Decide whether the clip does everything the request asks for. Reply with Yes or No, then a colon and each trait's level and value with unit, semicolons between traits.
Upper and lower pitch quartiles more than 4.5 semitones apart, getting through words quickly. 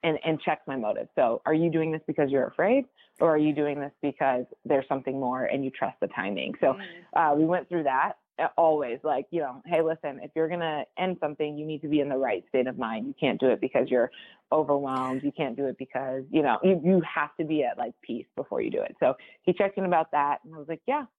No: average, 3.0 semitones; fast, 260 wpm